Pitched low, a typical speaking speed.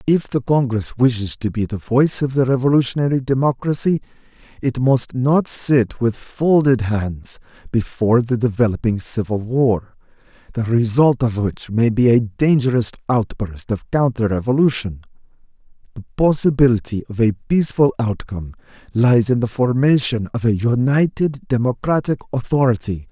No: low, 120 Hz; slow, 130 wpm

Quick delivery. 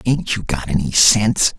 No: average, 190 wpm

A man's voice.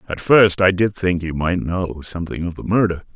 Yes: male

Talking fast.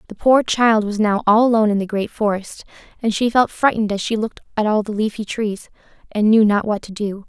Yes: fast, 240 wpm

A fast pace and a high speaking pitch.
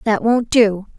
No: average, 185 wpm; high, 220 Hz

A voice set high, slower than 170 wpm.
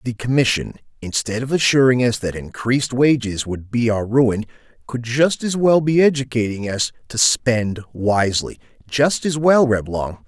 No: low, 120 Hz; average, 160 wpm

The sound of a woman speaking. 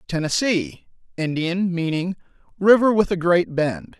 No: male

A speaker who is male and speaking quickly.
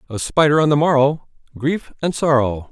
No: male; average, 175 wpm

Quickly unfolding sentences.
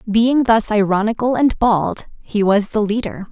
No: average, 165 wpm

